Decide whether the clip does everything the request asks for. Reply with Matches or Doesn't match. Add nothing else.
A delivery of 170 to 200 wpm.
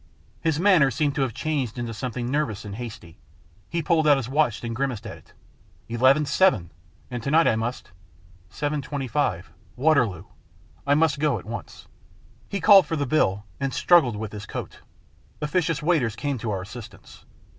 Matches